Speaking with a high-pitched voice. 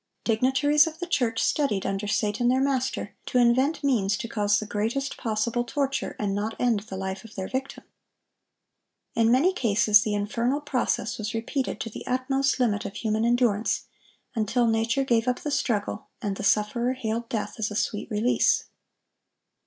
Yes: high, 230 Hz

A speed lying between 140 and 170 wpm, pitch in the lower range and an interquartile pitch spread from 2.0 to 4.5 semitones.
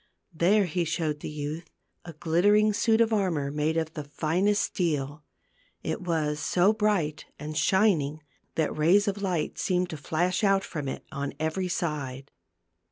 No: average, 160 wpm; medium, 165 Hz; average, 4.2 semitones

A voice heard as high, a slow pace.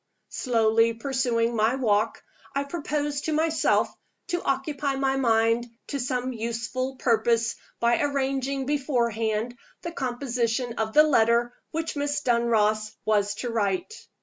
Yes: high, 245 Hz; slow, 125 wpm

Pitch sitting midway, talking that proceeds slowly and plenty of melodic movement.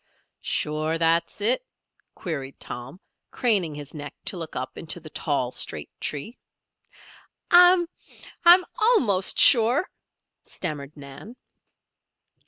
Yes: medium, 165 Hz; slow, 105 wpm; wide, 8.4 semitones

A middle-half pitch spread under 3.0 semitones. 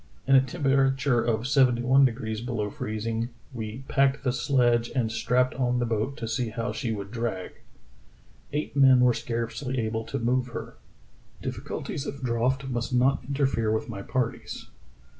Yes: narrow, 2.6 semitones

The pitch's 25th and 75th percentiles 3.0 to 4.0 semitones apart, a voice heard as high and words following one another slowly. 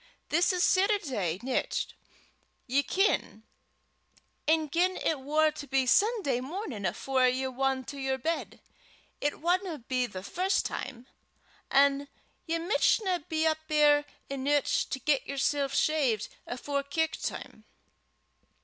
Yes: average, 3.6 semitones; very high, 285 Hz; slow, 130 wpm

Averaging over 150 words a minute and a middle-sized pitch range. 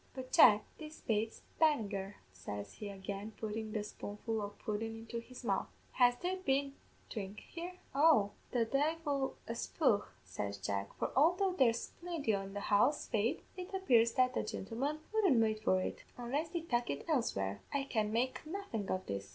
No: average, 170 wpm; wide, 5.8 semitones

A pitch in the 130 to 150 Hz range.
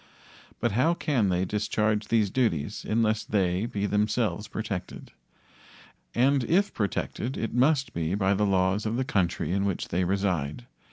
No: low, 105 Hz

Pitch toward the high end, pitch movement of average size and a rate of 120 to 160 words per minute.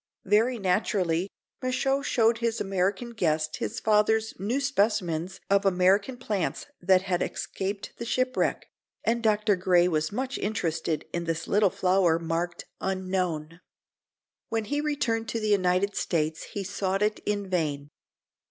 Yes: high, 195 Hz; average, 3.8 semitones; average, 140 wpm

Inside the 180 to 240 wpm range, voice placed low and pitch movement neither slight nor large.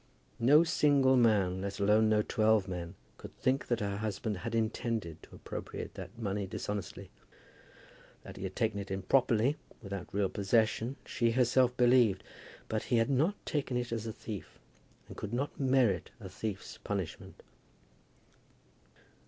No: average, 150 wpm; low, 110 Hz; average, 3.7 semitones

